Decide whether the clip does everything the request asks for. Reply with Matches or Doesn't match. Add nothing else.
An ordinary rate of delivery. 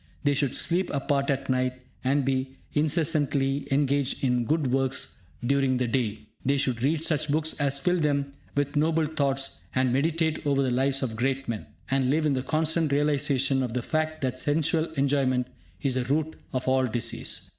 Matches